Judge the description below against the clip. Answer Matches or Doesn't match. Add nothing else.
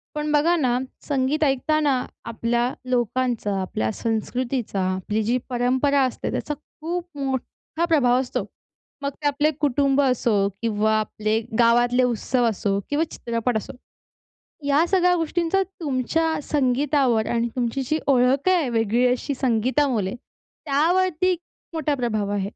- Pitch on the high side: Matches